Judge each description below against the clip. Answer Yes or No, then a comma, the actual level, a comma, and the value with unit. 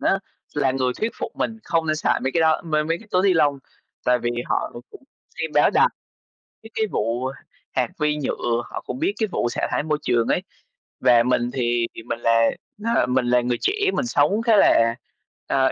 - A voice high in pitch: No, low, 135 Hz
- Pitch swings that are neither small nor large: No, wide, 6.1 semitones